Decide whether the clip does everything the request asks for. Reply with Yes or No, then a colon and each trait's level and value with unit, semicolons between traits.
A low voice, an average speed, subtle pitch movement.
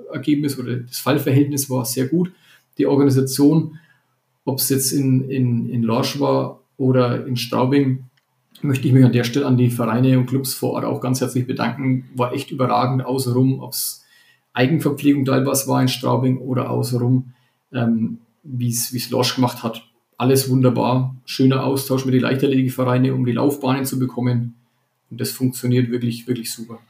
Yes: low, 130 Hz; average, 175 wpm; narrow, 1.5 semitones